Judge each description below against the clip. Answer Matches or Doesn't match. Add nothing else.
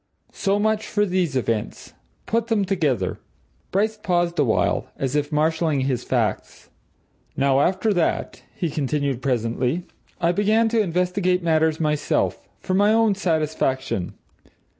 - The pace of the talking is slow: Matches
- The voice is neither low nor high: Matches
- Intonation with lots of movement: Matches